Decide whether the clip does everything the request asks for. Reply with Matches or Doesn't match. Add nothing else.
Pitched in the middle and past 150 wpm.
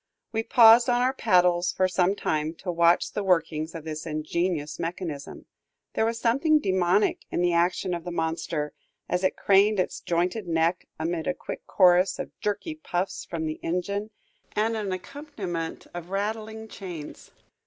Matches